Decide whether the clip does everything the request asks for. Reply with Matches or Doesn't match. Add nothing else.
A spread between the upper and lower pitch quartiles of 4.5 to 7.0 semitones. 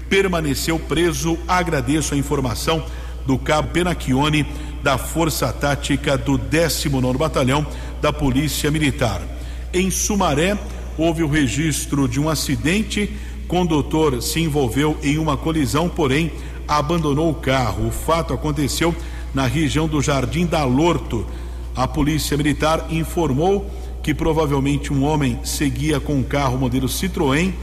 Doesn't match